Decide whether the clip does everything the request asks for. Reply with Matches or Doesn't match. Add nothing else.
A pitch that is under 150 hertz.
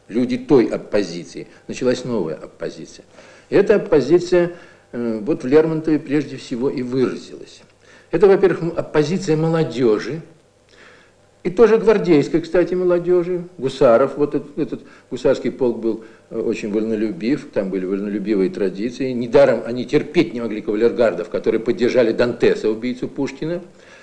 Matches